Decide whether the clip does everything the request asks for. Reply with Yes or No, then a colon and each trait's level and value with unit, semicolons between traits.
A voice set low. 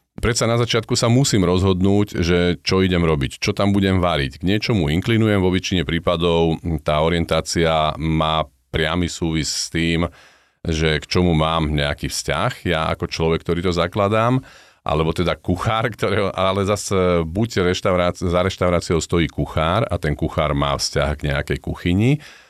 Yes: very low, 90 Hz